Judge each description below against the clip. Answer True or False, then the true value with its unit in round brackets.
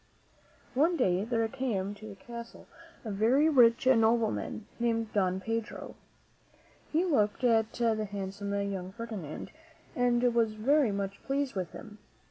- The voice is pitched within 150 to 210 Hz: False (225 Hz)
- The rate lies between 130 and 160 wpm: True (135 wpm)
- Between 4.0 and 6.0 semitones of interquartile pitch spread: False (3.2 semitones)